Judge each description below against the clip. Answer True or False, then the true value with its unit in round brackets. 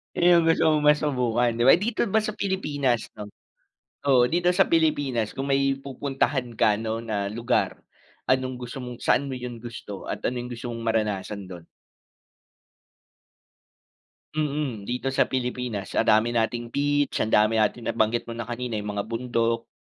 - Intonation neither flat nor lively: True (3.7 semitones)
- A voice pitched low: True (125 Hz)